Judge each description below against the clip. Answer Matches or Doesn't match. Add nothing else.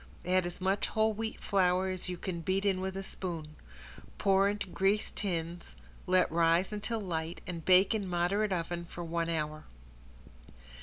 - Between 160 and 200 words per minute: Matches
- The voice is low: Doesn't match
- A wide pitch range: Doesn't match